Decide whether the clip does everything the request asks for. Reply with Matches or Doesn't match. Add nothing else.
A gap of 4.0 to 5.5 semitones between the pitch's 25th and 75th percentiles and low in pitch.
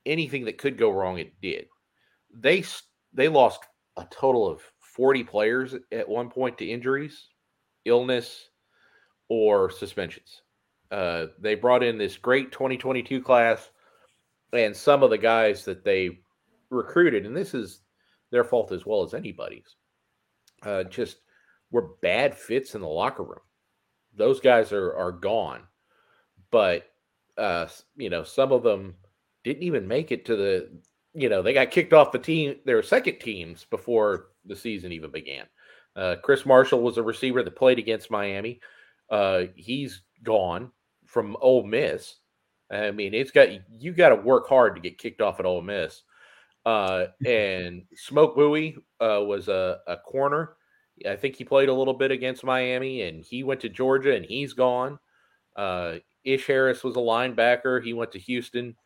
Matches